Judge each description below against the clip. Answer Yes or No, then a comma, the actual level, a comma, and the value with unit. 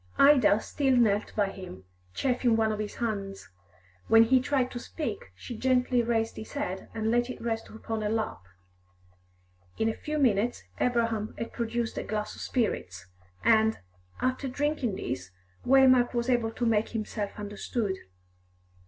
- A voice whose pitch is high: Yes, high, 225 Hz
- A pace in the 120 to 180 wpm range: Yes, average, 155 wpm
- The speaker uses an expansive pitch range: No, average, 2.9 semitones